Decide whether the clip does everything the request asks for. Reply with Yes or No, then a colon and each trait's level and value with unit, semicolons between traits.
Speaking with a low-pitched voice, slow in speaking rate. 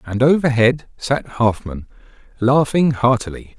Yes: low, 125 Hz; slow, 100 wpm